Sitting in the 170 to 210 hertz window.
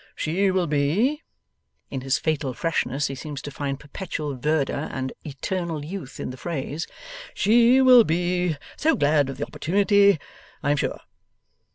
No: medium, 155 Hz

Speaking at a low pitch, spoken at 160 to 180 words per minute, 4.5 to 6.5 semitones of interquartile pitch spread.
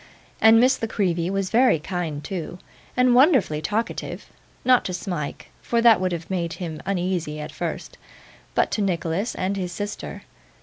No: medium, 185 Hz; average, 165 wpm; average, 4.8 semitones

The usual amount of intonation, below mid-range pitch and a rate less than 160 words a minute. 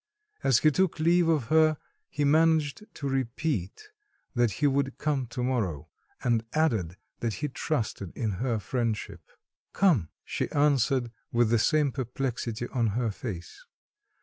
Yes: average, 4.9 semitones; low, 130 Hz; average, 145 wpm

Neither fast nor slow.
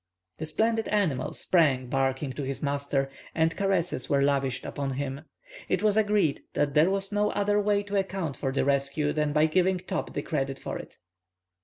Yes: average, 185 wpm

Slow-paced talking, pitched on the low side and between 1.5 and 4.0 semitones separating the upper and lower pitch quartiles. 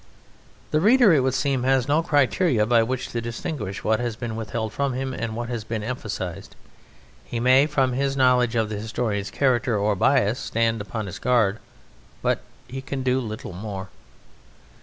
No: average, 180 wpm; low, 120 Hz; average, 3.3 semitones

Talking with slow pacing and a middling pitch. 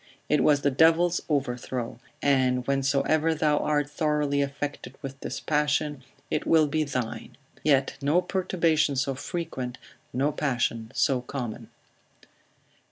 Yes: slow, 125 wpm; medium, 145 Hz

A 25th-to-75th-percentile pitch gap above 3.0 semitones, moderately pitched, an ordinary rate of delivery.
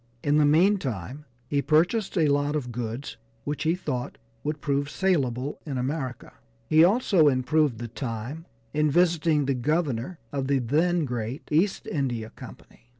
Yes: average, 4.0 semitones; medium, 145 Hz; average, 150 wpm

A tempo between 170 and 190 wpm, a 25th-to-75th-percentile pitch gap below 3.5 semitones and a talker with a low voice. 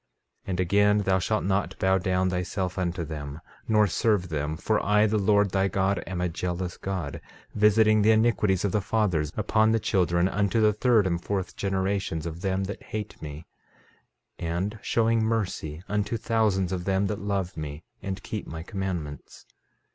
Yes: average, 175 wpm; average, 2.9 semitones; very low, 95 Hz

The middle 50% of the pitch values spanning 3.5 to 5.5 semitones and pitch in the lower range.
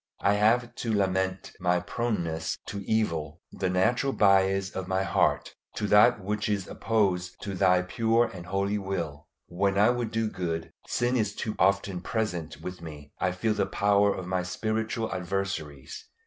No: average, 2.9 semitones; very low, 95 Hz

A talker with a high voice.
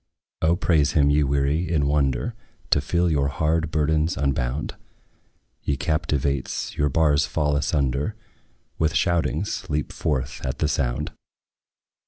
No: very low, 75 Hz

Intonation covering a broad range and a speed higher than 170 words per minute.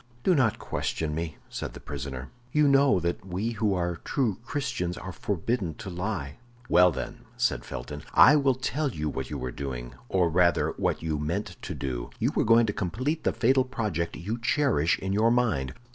Yes: wide, 7.1 semitones; average, 190 wpm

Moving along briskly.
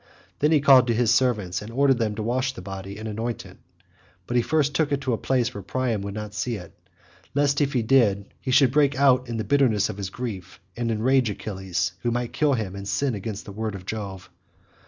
Yes: fast, 240 wpm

